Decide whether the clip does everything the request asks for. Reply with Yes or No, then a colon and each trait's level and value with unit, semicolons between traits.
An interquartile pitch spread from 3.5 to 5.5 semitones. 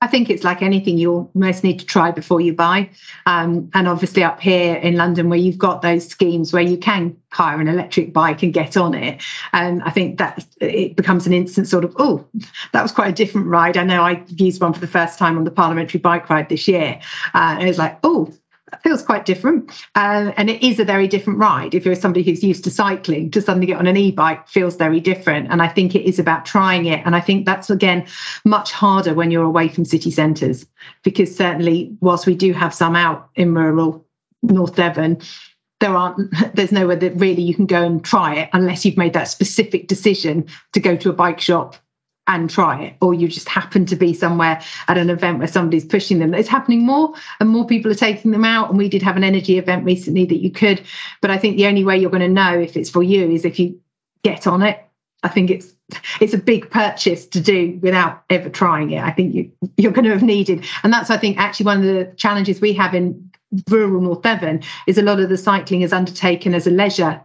No: narrow, 2.6 semitones